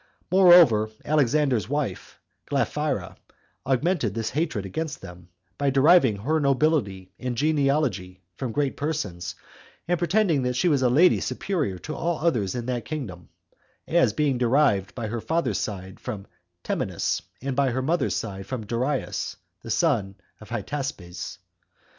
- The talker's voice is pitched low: Yes, low, 130 Hz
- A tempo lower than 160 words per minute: Yes, average, 140 wpm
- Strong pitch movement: Yes, wide, 6.3 semitones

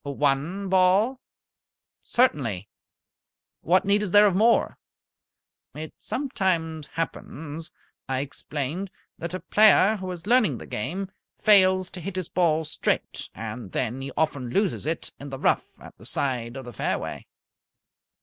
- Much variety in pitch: Yes, wide, 5.7 semitones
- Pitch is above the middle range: No, medium, 165 Hz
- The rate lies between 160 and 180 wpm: No, average, 140 wpm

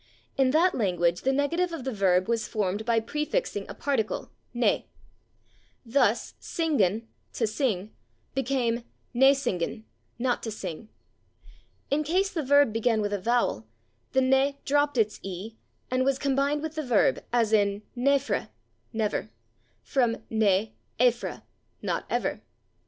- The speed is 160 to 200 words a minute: No, average, 140 wpm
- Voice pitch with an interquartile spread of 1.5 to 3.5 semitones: No, average, 4.5 semitones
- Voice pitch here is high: Yes, high, 240 Hz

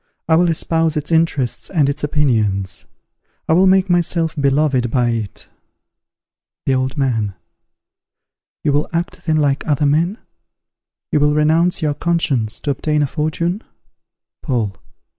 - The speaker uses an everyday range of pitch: Yes, average, 3.8 semitones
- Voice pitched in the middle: Yes, medium, 150 Hz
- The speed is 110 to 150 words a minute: Yes, average, 140 wpm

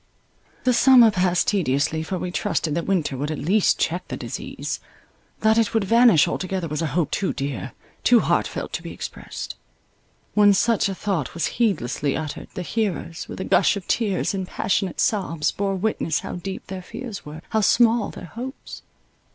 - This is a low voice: No, high, 190 Hz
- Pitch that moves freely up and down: No, average, 4.9 semitones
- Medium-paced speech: Yes, average, 180 wpm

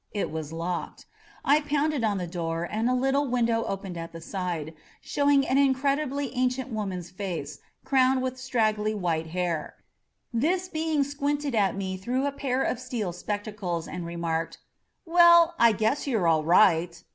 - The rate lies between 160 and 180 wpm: Yes, average, 165 wpm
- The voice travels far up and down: Yes, wide, 7.4 semitones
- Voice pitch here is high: Yes, high, 220 Hz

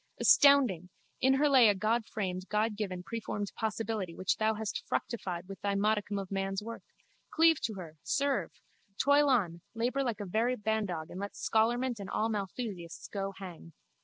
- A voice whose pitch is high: Yes, high, 210 Hz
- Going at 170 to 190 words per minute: No, average, 160 wpm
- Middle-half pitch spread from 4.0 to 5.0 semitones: No, average, 3.4 semitones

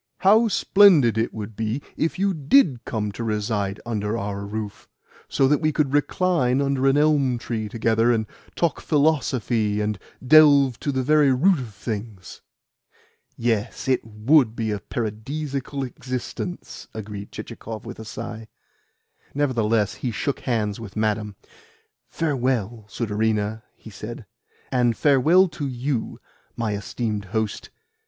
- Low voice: Yes, low, 120 Hz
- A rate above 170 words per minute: No, slow, 135 wpm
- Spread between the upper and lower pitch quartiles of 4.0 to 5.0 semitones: Yes, average, 4.6 semitones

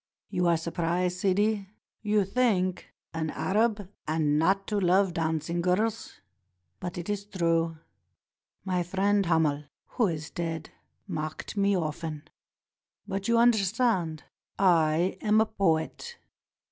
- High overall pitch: No, medium, 180 Hz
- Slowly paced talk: Yes, slow, 120 wpm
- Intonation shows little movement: No, average, 3.8 semitones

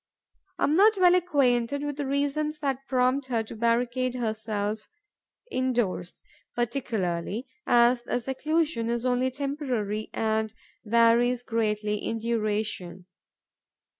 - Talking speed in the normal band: No, slow, 115 wpm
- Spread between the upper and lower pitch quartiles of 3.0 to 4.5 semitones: Yes, average, 3.8 semitones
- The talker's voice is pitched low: No, high, 240 Hz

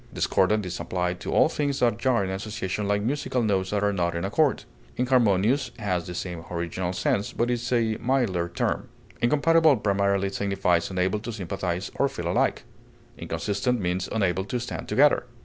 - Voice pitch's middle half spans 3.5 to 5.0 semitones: Yes, average, 4.6 semitones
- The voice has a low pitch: Yes, low, 100 Hz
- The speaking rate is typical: Yes, average, 170 wpm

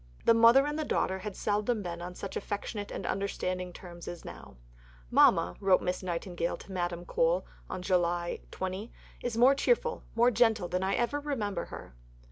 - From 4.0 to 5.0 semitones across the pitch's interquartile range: Yes, average, 4.6 semitones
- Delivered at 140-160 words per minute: No, average, 170 wpm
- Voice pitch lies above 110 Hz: Yes, high, 190 Hz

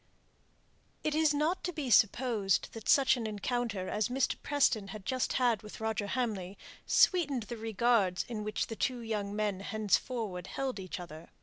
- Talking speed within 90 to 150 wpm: No, average, 170 wpm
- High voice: Yes, high, 220 Hz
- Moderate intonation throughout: Yes, average, 4.0 semitones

